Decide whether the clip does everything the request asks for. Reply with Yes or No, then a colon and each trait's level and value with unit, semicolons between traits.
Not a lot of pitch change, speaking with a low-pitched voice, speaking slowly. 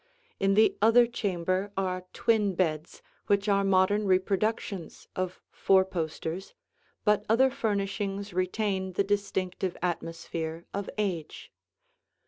No: narrow, 2.0 semitones; high, 195 Hz; slow, 110 wpm